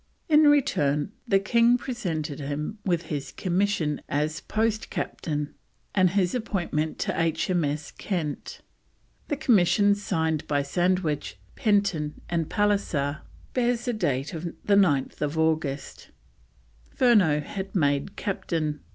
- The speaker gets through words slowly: Yes, slow, 110 wpm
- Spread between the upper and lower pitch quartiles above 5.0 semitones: Yes, wide, 5.4 semitones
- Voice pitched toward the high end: No, medium, 175 Hz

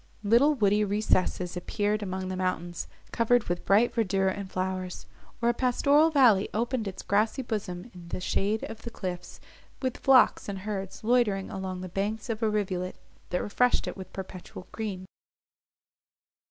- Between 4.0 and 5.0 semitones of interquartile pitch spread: No, average, 3.4 semitones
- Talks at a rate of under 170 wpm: Yes, average, 160 wpm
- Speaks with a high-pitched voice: Yes, high, 200 Hz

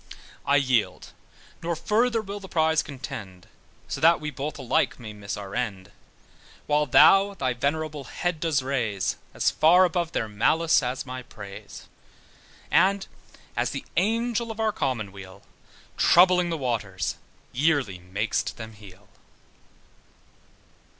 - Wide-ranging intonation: Yes, wide, 8.0 semitones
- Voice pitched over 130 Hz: Yes, medium, 140 Hz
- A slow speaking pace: Yes, slow, 130 wpm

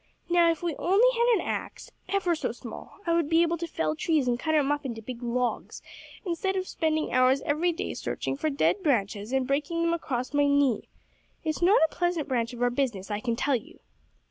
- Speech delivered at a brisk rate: Yes, fast, 220 wpm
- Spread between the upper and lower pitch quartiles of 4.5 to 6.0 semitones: Yes, average, 5.2 semitones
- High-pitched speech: Yes, very high, 290 Hz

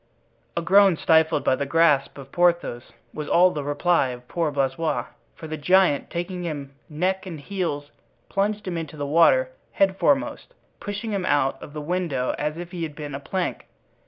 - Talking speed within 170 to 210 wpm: Yes, average, 180 wpm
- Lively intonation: No, average, 4.2 semitones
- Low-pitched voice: No, medium, 165 Hz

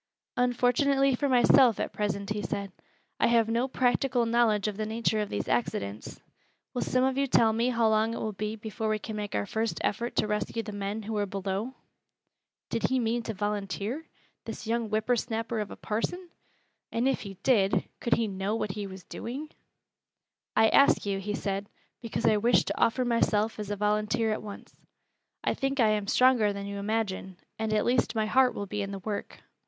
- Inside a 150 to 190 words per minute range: No, average, 200 wpm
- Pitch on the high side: Yes, high, 220 Hz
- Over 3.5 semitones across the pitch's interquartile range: No, narrow, 2.5 semitones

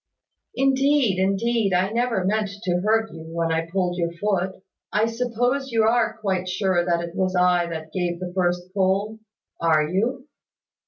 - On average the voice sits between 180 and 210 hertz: Yes, high, 190 Hz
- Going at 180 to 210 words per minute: No, average, 165 wpm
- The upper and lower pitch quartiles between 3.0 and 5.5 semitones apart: Yes, average, 4.1 semitones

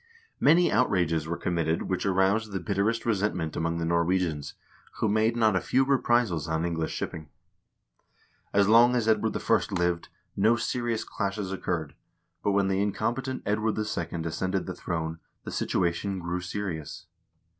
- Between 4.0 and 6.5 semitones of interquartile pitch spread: Yes, average, 4.5 semitones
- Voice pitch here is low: Yes, very low, 95 Hz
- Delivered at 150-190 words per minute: Yes, average, 155 wpm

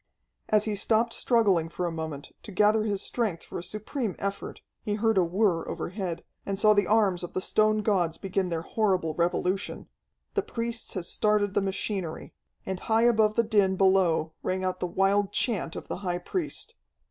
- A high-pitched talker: Yes, high, 195 Hz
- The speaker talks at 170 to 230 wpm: Yes, average, 185 wpm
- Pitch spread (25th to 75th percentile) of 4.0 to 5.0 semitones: No, average, 3.1 semitones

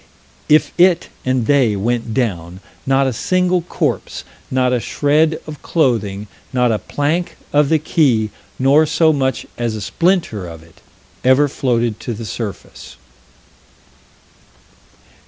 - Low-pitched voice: Yes, low, 130 Hz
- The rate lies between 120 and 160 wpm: Yes, slow, 135 wpm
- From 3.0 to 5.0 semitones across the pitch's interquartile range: No, wide, 5.5 semitones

